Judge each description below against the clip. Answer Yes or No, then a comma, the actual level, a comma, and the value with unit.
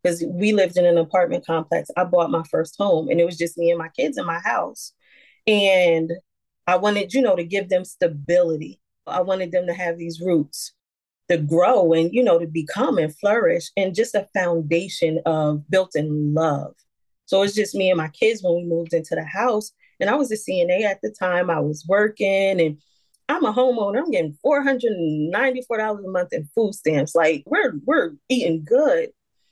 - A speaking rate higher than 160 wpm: Yes, average, 200 wpm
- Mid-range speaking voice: Yes, medium, 180 Hz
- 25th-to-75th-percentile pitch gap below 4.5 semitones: Yes, average, 3.8 semitones